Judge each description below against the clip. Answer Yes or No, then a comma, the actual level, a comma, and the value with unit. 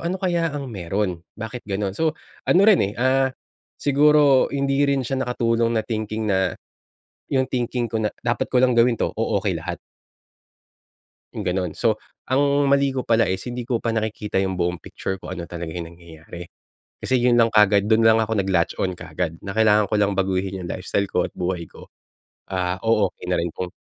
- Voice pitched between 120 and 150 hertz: No, low, 110 Hz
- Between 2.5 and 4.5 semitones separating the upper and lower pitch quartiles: No, average, 5.1 semitones